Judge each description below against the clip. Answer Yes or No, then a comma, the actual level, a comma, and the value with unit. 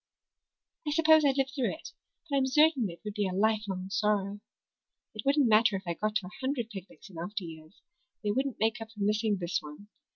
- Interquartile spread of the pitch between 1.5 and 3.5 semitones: No, average, 5.2 semitones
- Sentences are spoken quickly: Yes, fast, 215 wpm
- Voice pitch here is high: Yes, high, 215 Hz